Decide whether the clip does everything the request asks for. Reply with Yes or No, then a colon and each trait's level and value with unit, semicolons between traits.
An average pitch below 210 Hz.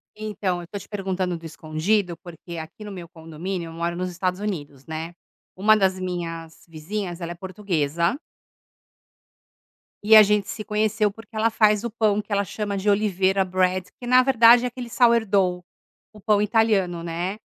Yes: high, 190 Hz